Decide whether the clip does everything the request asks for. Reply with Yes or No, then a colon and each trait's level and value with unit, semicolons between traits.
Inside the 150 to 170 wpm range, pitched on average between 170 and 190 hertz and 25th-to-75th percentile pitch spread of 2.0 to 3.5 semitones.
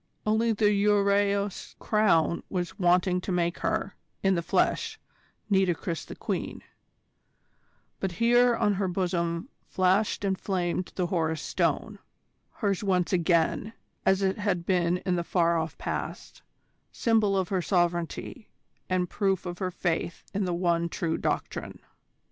No: average, 140 wpm; medium, 185 Hz; narrow, 2.6 semitones